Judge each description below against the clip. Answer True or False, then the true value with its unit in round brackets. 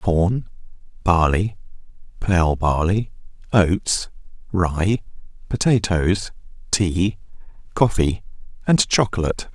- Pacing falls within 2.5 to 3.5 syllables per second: True (3.4 syllables/s)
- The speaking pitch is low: True (95 Hz)